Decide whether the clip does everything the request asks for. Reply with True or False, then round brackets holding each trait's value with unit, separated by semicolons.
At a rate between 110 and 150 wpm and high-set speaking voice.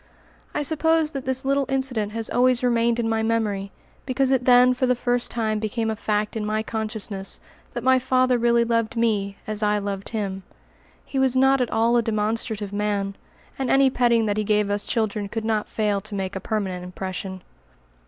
False (195 wpm; 225 Hz)